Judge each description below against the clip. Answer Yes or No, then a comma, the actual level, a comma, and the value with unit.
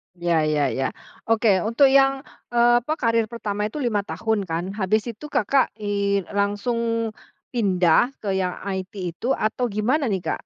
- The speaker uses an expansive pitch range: No, average, 3.7 semitones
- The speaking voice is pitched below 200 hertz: No, high, 215 Hz